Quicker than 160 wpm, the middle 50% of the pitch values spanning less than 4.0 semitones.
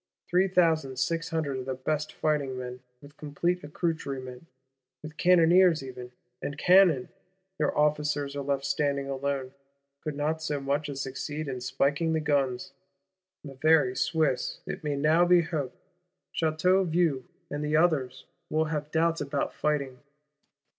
No: average, 145 wpm; average, 2.8 semitones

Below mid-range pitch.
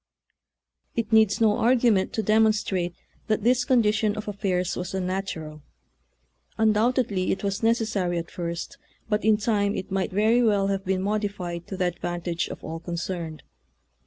No: high, 200 Hz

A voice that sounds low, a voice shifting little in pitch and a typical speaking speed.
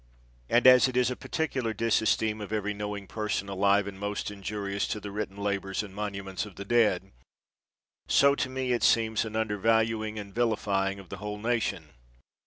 Yes: low, 105 Hz; narrow, 2.2 semitones; average, 180 wpm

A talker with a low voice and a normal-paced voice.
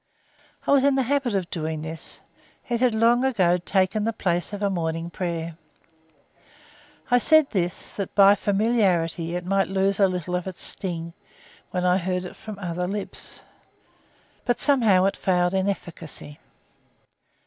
No: high, 190 Hz; average, 160 wpm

